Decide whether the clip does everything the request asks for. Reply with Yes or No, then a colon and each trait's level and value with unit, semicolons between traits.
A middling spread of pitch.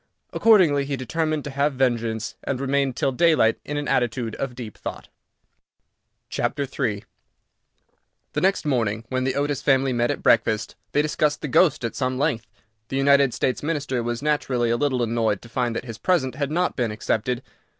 Yes: average, 3.4 semitones